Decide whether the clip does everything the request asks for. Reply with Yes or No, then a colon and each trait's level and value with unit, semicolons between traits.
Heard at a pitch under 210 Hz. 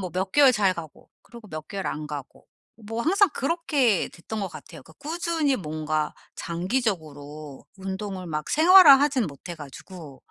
Yes: high, 190 Hz